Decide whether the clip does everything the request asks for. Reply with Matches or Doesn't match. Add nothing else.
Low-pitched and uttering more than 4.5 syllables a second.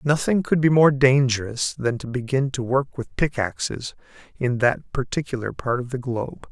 Matches